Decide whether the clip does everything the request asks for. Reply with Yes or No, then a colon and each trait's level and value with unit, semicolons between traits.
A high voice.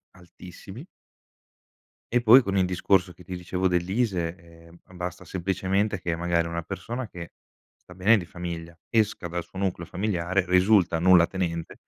No: very low, 90 Hz